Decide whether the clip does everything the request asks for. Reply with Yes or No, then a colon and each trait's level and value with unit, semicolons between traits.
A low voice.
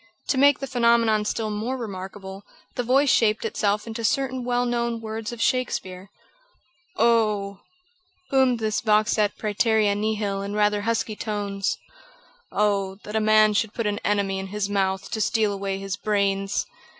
No: high, 215 Hz